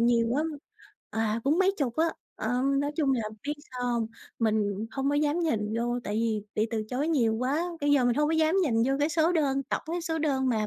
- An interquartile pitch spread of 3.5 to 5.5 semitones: Yes, average, 4.9 semitones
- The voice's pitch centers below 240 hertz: No, very high, 265 Hz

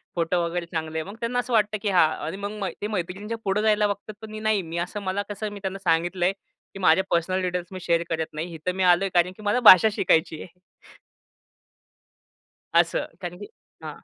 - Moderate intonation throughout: Yes, average, 3.3 semitones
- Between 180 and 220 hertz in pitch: Yes, medium, 185 Hz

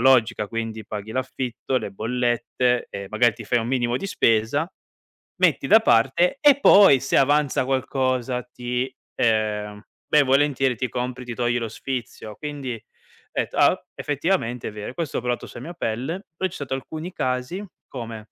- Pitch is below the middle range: Yes, low, 125 Hz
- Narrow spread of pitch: No, average, 3.1 semitones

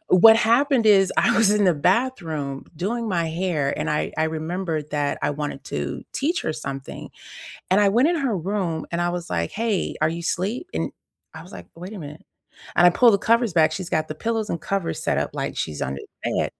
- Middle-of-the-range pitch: Yes, medium, 180 Hz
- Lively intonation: Yes, wide, 5.7 semitones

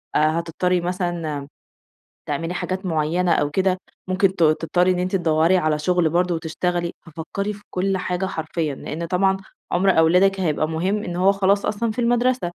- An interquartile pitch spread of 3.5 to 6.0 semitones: No, average, 2.8 semitones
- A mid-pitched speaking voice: Yes, medium, 180 Hz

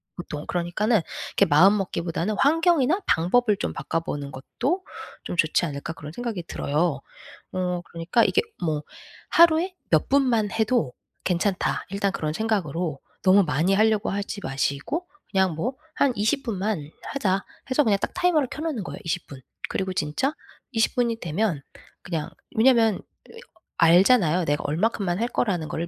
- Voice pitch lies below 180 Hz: No, high, 195 Hz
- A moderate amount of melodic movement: No, wide, 6.0 semitones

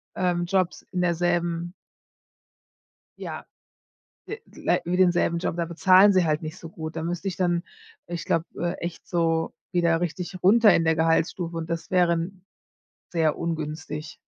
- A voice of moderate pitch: Yes, medium, 170 Hz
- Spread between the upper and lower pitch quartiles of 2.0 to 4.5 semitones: No, narrow, 1.5 semitones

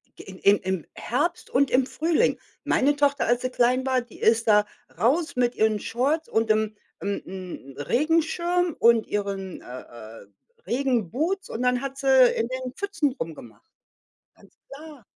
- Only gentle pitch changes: No, average, 4.9 semitones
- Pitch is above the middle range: Yes, very high, 250 Hz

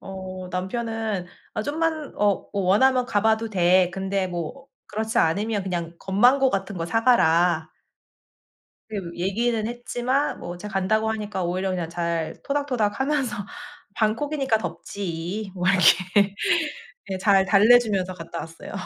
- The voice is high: Yes, high, 200 Hz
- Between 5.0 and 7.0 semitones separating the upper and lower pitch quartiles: No, average, 3.9 semitones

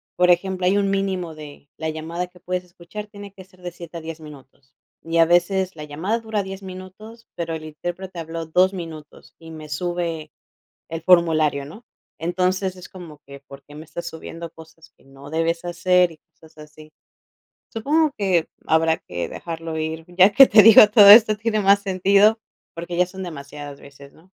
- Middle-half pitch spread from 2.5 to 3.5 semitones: Yes, average, 3.1 semitones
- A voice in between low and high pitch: Yes, medium, 170 Hz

